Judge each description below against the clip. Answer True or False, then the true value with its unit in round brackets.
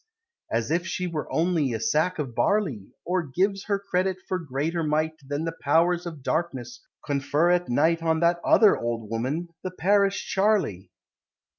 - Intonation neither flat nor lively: True (4.3 semitones)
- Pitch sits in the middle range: True (165 Hz)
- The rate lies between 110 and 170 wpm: True (165 wpm)